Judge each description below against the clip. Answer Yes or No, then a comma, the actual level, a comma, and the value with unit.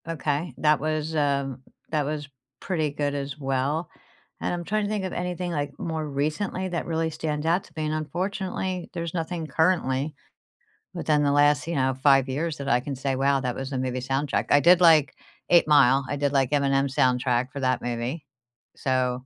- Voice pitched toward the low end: No, medium, 145 Hz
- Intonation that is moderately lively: Yes, average, 3.2 semitones